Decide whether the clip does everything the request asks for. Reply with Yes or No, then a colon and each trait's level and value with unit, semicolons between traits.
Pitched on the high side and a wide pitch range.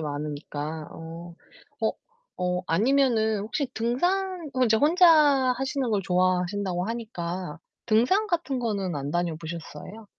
Yes: high, 200 Hz; wide, 6.9 semitones